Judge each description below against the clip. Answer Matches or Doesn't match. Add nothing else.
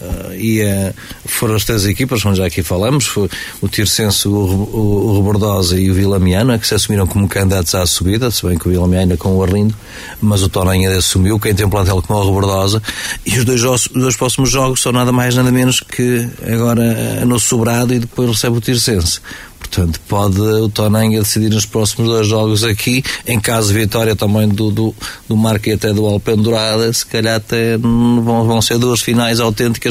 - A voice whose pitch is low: Matches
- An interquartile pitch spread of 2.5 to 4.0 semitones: Matches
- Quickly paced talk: Matches